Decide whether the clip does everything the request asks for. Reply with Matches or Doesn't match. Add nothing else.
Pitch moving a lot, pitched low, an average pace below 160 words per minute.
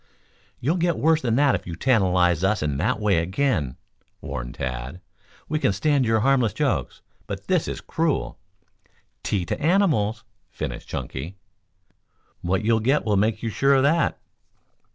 Doesn't match